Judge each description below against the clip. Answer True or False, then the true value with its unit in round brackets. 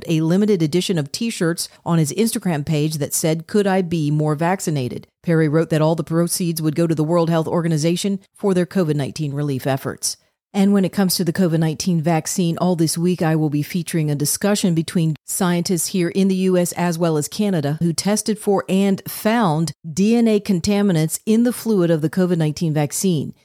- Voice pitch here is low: False (170 Hz)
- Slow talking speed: False (200 wpm)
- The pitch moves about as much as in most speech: True (3.4 semitones)